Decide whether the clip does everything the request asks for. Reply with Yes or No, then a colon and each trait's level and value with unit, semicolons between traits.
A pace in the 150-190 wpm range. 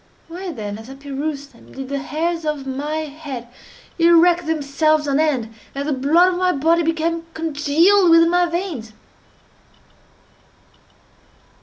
No: average, 140 wpm